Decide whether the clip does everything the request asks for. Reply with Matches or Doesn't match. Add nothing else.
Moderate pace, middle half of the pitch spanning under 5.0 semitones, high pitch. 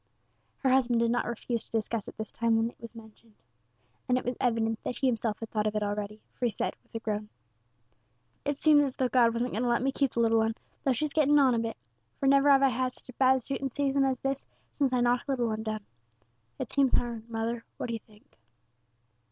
Doesn't match